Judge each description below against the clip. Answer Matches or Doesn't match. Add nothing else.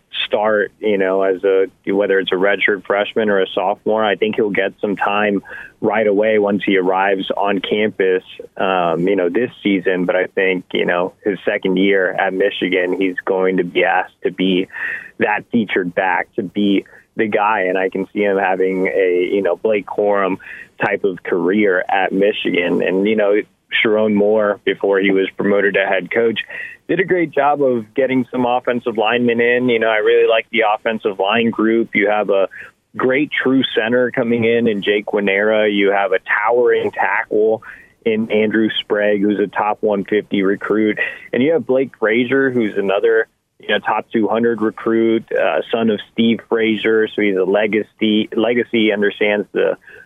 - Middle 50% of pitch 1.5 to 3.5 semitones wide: Matches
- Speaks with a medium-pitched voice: Doesn't match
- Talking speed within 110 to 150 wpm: Doesn't match